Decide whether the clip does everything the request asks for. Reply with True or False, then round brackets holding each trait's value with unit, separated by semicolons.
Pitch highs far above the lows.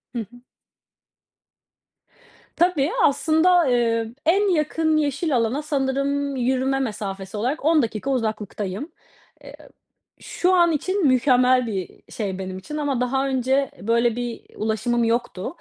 False (4.6 semitones)